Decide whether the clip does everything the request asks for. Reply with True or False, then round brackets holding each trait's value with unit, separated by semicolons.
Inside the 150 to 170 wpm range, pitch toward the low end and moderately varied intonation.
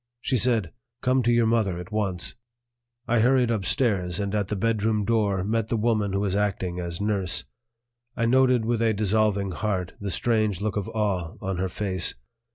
False (180 wpm; 105 Hz; 3.1 semitones)